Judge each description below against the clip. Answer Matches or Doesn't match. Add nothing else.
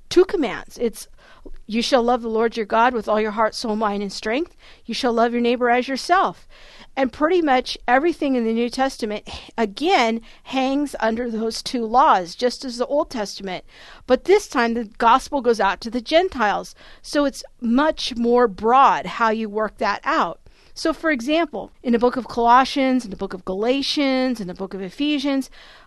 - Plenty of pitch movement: Doesn't match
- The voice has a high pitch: Matches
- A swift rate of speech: Doesn't match